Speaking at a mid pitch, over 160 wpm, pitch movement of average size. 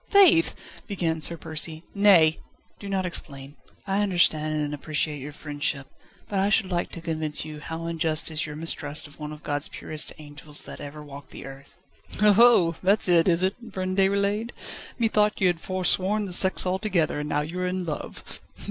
Yes: medium, 165 Hz; average, 185 wpm; average, 4.1 semitones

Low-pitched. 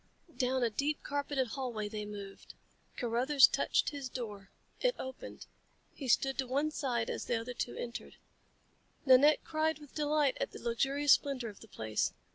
No: very high, 260 Hz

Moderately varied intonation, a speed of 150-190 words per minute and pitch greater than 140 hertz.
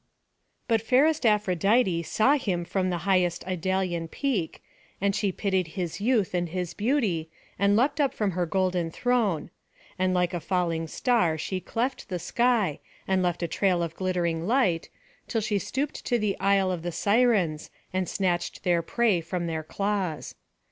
Yes: average, 4.0 semitones; average, 165 wpm; medium, 185 Hz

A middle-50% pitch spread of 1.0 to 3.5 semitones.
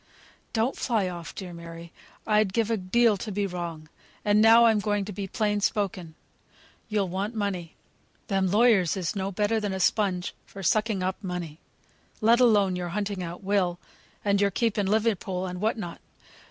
Yes: average, 2.9 semitones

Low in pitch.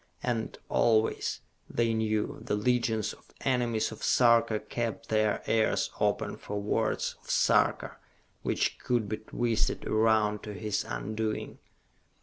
Yes: low, 110 Hz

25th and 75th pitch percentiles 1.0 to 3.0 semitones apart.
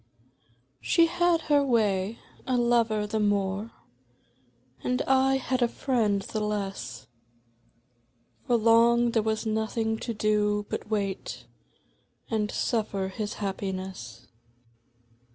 Yes: narrow, 2.6 semitones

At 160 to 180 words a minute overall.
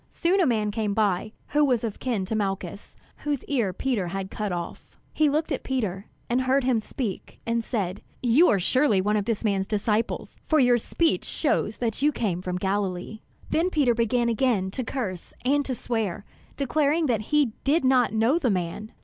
No: average, 190 wpm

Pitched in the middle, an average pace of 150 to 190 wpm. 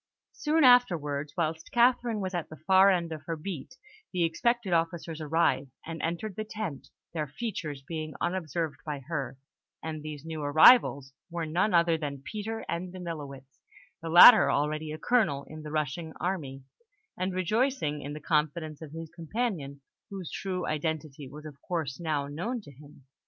Yes: medium, 160 Hz; average, 165 wpm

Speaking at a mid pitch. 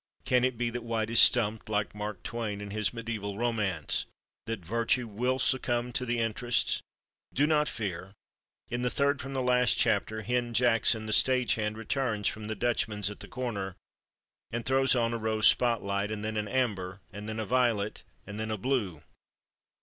No: low, 115 Hz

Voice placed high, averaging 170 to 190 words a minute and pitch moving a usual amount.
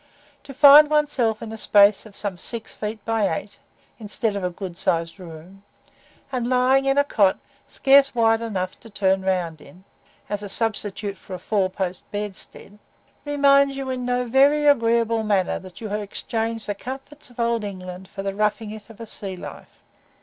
Yes: high, 215 Hz; average, 185 wpm; average, 4.1 semitones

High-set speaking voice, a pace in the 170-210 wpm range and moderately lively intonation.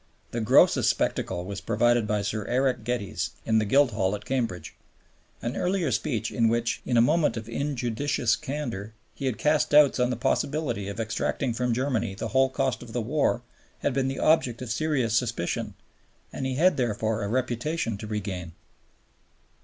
No: low, 120 Hz; average, 175 wpm; average, 3.6 semitones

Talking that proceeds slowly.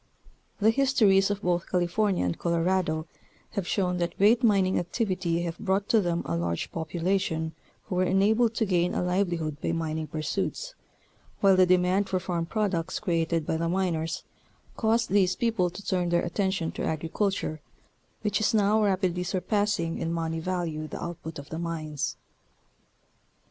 No: average, 160 wpm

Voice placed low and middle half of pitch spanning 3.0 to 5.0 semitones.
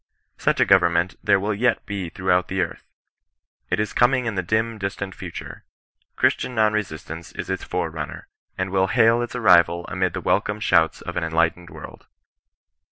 Yes: very low, 95 Hz; average, 3.7 semitones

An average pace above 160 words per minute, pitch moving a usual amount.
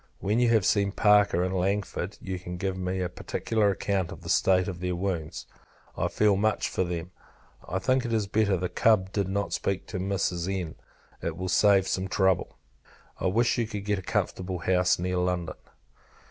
No: average, 195 wpm; narrow, 2.0 semitones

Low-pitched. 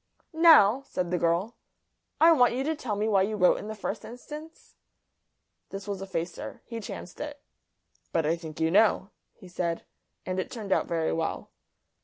No: high, 200 Hz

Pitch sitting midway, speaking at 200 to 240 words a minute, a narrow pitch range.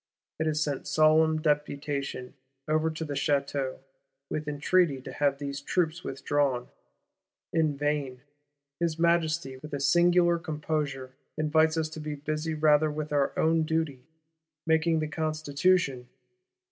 No: medium, 155 Hz; slow, 135 wpm; narrow, 2.1 semitones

